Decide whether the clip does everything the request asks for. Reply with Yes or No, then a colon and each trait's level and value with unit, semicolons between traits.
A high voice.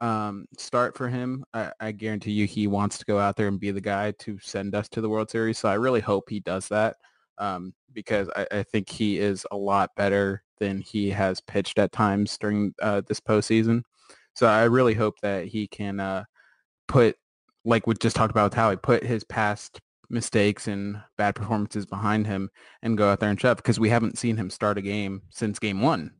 No: low, 105 Hz